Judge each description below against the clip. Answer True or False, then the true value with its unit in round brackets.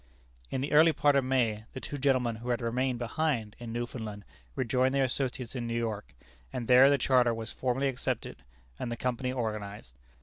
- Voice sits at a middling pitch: False (125 Hz)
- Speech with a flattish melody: True (2.3 semitones)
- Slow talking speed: False (190 wpm)